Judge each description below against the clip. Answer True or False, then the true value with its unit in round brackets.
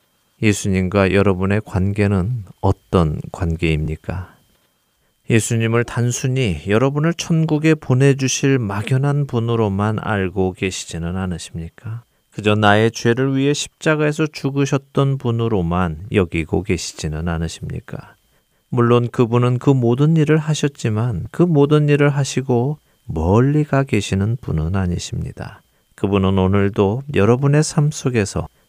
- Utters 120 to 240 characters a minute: False (285 characters per minute)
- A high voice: False (115 Hz)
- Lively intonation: True (6.2 semitones)